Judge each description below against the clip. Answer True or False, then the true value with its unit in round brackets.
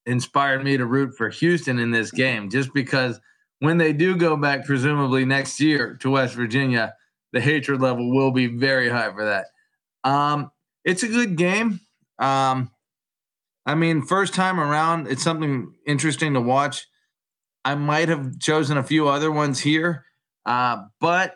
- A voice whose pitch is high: False (140 Hz)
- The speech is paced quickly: False (165 wpm)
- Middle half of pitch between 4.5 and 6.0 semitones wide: False (3.7 semitones)